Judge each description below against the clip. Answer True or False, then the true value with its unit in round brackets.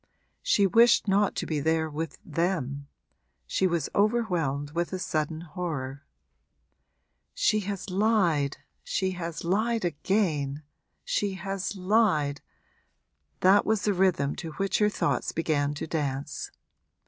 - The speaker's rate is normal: False (125 wpm)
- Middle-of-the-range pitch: True (175 Hz)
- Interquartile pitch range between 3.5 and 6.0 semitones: True (4.9 semitones)